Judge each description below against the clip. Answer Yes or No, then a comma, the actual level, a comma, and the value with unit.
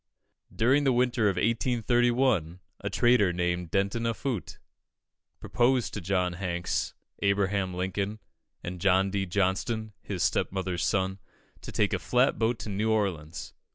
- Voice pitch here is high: No, low, 100 Hz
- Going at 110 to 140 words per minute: Yes, slow, 135 wpm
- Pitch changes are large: No, average, 4.1 semitones